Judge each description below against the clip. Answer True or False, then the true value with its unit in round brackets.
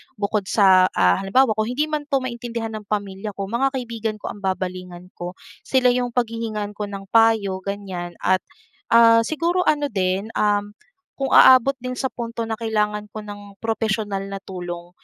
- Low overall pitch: False (210 Hz)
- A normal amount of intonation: True (3.2 semitones)